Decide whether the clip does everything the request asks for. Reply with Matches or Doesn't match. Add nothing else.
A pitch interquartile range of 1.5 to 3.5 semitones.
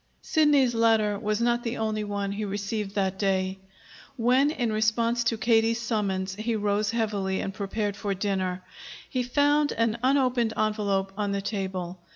Matches